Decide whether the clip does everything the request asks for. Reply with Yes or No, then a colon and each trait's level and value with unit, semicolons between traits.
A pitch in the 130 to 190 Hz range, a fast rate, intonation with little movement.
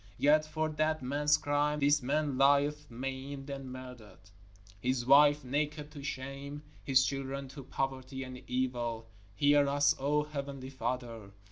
No: medium, 140 Hz; average, 140 wpm; narrow, 2.2 semitones